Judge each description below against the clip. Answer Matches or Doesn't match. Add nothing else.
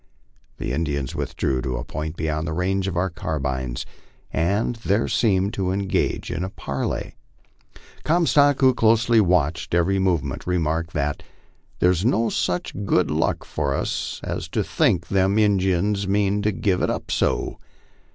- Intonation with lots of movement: Doesn't match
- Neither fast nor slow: Matches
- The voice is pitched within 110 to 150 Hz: Doesn't match